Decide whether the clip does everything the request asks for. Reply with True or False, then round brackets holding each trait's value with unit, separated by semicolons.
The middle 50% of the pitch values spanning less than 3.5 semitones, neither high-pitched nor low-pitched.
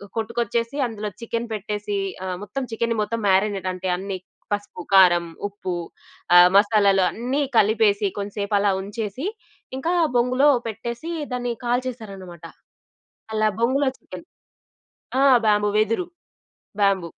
False (2.9 semitones; 210 Hz)